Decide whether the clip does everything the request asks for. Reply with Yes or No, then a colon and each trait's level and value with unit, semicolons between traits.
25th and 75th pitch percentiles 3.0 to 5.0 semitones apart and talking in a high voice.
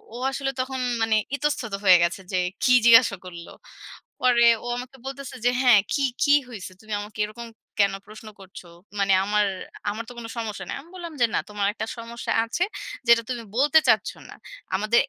Yes: average, 3.7 semitones; high, 230 Hz